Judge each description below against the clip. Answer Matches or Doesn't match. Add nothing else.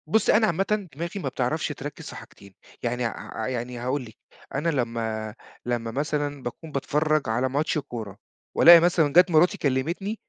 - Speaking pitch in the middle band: Matches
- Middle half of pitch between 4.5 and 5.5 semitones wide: Matches